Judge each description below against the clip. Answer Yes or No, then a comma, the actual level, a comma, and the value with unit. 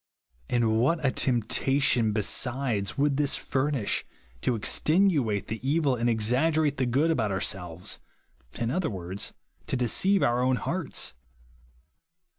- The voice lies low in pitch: Yes, low, 125 Hz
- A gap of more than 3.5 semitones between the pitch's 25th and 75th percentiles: Yes, average, 4.9 semitones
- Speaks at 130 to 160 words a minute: Yes, slow, 135 wpm